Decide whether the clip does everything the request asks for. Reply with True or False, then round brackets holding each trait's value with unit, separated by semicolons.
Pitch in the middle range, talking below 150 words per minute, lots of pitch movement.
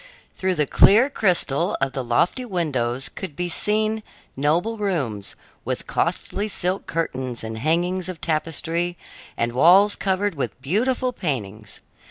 True (170 Hz; 135 wpm; 6.6 semitones)